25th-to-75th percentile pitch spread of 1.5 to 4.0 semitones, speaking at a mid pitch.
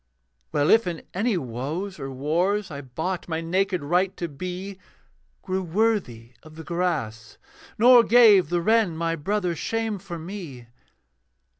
No: average, 4.6 semitones; medium, 175 Hz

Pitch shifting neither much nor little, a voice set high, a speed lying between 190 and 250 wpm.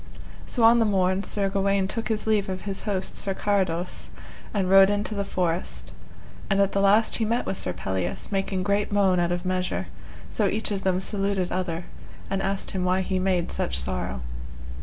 No: narrow, 1.8 semitones; high, 195 Hz; average, 195 wpm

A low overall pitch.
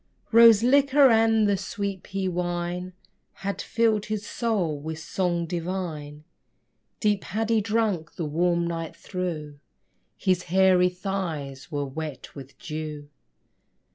No: medium, 180 Hz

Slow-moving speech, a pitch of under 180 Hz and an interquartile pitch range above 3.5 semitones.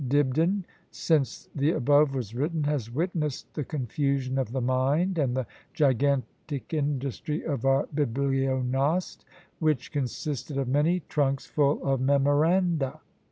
No: slow, 125 wpm; medium, 140 Hz; narrow, 2.5 semitones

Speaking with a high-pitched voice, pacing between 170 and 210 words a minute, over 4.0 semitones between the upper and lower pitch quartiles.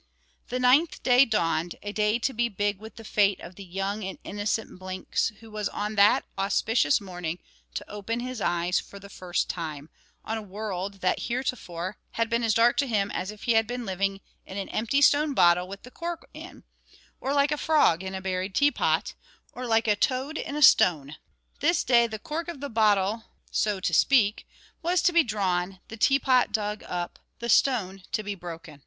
Yes: high, 210 Hz; average, 200 wpm; average, 4.5 semitones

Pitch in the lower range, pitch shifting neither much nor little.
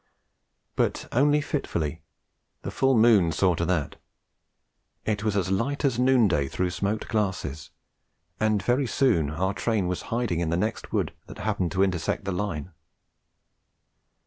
Yes: low, 100 Hz; average, 4.9 semitones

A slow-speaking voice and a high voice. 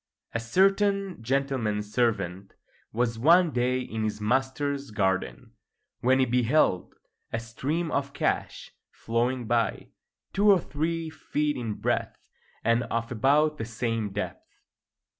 No: slow, 125 wpm; low, 125 Hz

